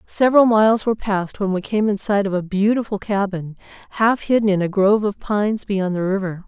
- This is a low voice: No, high, 205 Hz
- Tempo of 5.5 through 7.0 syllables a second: Yes, 5.8 syllables/s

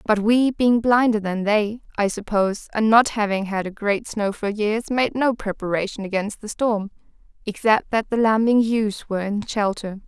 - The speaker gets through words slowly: No, average, 185 wpm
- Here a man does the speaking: No, female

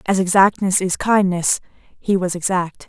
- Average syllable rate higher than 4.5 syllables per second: No, 4.2 syllables/s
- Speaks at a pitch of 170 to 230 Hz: Yes, medium, 185 Hz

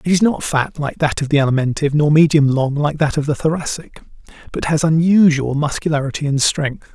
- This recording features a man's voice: Yes, male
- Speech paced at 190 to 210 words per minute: Yes, average, 200 wpm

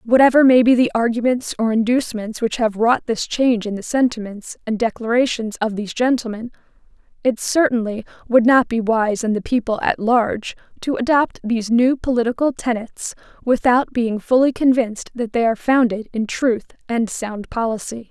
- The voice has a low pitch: No, high, 235 Hz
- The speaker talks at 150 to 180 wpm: Yes, average, 165 wpm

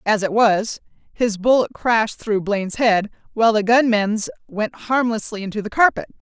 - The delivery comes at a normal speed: Yes, average, 160 wpm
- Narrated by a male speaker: No, female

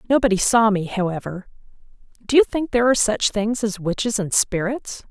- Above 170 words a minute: No, average, 165 wpm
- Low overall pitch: No, high, 215 Hz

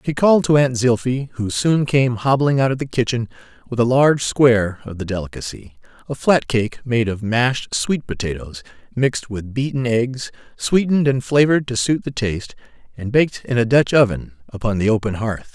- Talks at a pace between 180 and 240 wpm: Yes, average, 185 wpm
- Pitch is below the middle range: Yes, low, 120 Hz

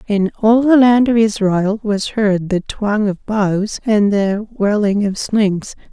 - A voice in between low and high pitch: No, high, 210 Hz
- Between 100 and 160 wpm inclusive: No, average, 170 wpm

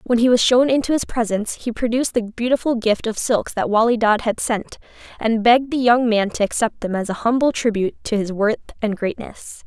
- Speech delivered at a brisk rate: Yes, fast, 225 wpm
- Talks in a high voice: Yes, high, 230 Hz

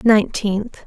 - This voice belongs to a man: No, female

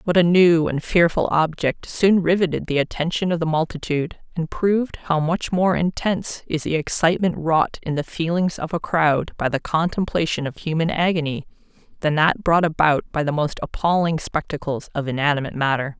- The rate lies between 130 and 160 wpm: No, average, 175 wpm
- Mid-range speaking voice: Yes, medium, 160 Hz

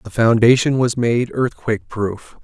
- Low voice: Yes, low, 120 Hz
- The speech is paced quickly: No, average, 150 wpm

